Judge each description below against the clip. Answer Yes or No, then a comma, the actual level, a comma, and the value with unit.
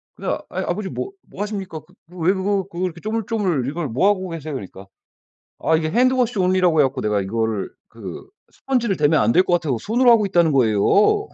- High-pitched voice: No, medium, 180 Hz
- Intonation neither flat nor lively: No, wide, 5.8 semitones